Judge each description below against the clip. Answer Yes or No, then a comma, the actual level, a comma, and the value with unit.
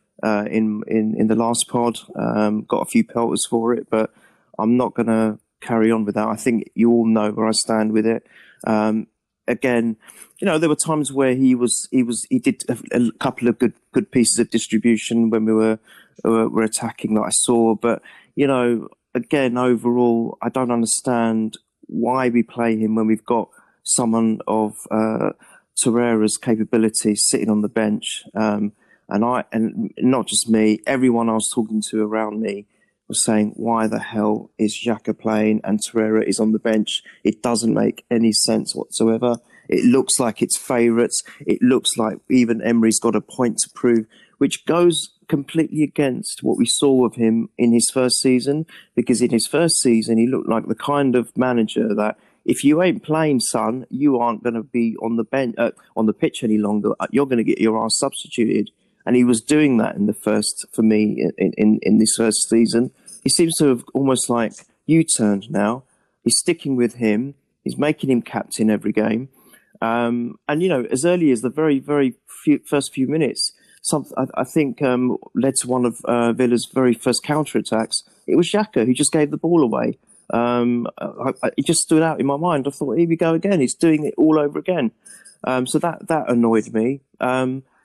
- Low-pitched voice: Yes, low, 120 Hz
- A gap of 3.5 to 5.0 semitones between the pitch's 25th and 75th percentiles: No, average, 3.0 semitones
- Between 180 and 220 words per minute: Yes, average, 200 wpm